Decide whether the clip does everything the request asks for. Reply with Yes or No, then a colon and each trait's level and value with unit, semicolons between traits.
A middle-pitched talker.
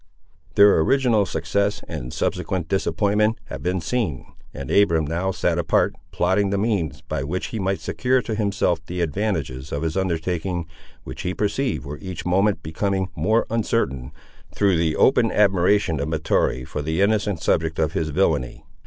No: very low, 95 Hz